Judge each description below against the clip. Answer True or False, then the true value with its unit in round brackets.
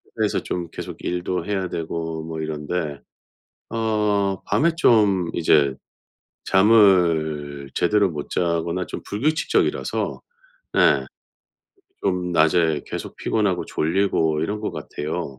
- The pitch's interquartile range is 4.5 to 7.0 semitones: False (4.1 semitones)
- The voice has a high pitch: False (90 Hz)